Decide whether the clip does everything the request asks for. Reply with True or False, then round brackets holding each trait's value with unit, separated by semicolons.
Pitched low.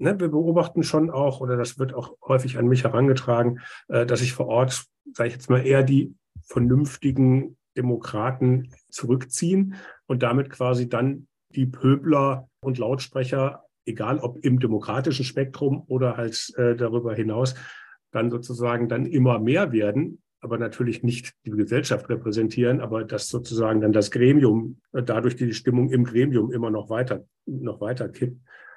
True (125 Hz)